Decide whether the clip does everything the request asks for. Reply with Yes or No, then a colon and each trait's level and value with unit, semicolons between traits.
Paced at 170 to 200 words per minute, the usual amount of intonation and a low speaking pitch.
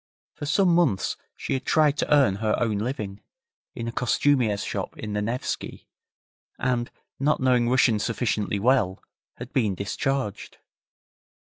No: average, 140 wpm; average, 4.4 semitones; low, 120 Hz